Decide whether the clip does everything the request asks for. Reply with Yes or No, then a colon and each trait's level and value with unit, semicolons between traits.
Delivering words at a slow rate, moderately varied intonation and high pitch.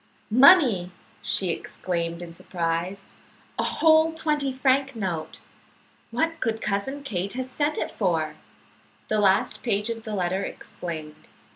No: slow, 130 wpm; wide, 7.2 semitones; high, 210 Hz